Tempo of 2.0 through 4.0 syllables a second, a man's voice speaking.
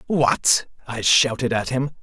Yes: 3.7 syllables/s; male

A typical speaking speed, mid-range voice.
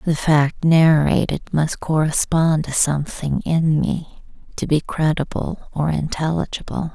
No: slow, 120 wpm; medium, 155 Hz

